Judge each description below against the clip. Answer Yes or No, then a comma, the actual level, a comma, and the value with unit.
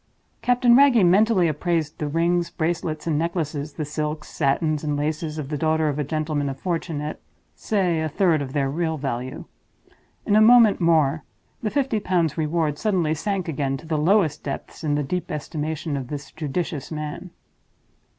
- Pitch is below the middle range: No, medium, 155 Hz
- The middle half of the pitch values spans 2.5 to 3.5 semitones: Yes, average, 2.9 semitones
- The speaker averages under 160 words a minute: No, average, 170 wpm